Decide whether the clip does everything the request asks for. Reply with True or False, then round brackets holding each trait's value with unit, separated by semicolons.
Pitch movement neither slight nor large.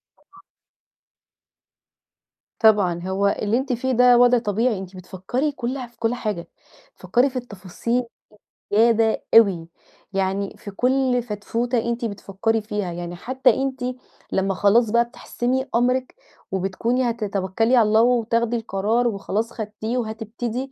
True (3.5 semitones)